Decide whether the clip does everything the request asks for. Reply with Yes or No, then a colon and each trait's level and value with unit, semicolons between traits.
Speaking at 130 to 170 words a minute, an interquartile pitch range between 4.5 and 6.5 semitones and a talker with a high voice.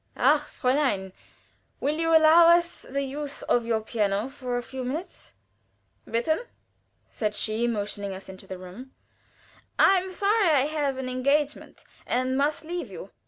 Yes: average, 155 wpm; wide, 5.4 semitones; very high, 265 Hz